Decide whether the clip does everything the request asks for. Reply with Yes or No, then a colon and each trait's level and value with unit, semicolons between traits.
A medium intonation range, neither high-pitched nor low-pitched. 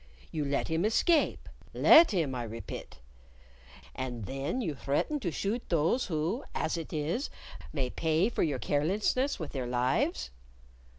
No: wide, 7.4 semitones; medium, 155 Hz